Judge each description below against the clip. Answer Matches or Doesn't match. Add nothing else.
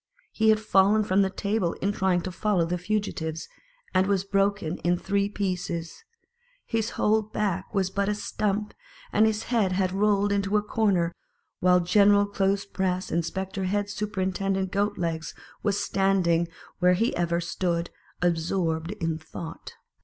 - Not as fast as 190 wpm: Matches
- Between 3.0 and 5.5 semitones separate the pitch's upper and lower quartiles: Doesn't match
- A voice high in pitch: Matches